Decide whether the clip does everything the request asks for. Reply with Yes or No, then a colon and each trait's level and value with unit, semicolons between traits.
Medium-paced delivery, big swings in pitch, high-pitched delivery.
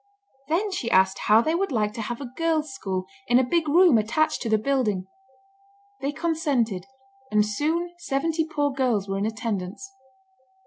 Yes: average, 170 wpm; wide, 6.9 semitones; very high, 260 Hz